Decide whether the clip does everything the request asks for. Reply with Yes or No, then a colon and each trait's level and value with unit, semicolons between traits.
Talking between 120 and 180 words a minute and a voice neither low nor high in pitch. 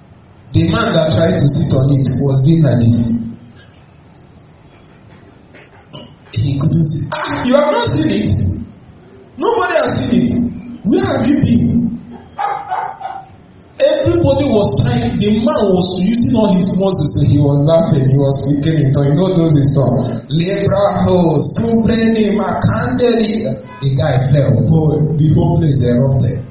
Yes: average, 160 wpm; medium, 155 Hz